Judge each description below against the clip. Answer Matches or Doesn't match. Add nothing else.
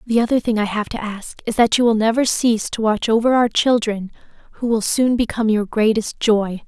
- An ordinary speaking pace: Doesn't match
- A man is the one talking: Doesn't match